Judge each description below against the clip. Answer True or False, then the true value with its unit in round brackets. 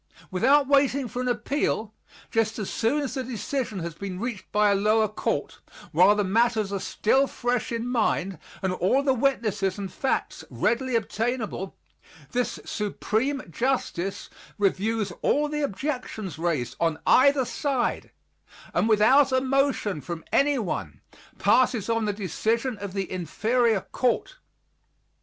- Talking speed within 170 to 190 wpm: False (140 wpm)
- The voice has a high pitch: True (225 Hz)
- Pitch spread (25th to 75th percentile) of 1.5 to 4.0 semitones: False (4.8 semitones)